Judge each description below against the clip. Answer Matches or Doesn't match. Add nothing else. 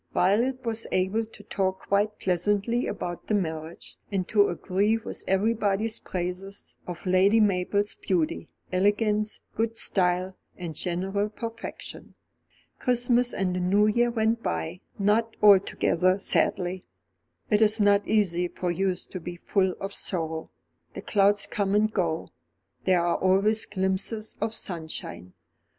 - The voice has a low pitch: Doesn't match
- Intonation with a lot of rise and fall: Doesn't match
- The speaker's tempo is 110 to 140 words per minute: Matches